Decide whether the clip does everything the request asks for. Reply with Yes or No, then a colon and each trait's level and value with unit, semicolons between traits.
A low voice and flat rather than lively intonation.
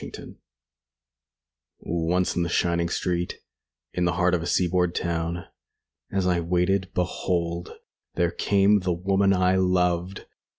Yes: very low, 90 Hz; narrow, 1.3 semitones